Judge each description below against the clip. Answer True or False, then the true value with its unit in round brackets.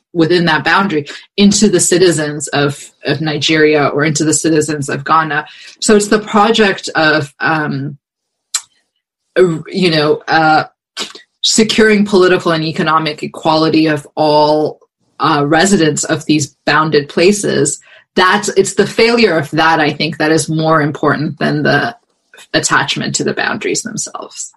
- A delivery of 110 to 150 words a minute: True (135 wpm)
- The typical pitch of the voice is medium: True (160 Hz)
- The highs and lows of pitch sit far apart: False (3.4 semitones)